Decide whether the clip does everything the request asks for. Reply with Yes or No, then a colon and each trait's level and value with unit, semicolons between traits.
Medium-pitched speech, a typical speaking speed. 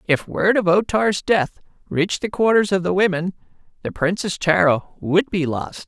Yes: medium, 180 Hz; average, 185 wpm